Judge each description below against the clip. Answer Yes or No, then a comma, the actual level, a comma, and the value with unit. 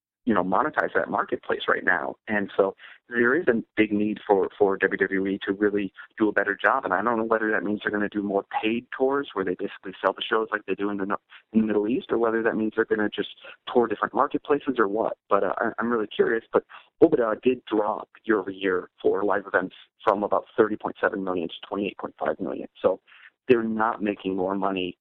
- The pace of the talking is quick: Yes, fast, 220 wpm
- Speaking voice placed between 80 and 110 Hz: Yes, low, 105 Hz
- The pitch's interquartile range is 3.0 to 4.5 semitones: No, narrow, 2.5 semitones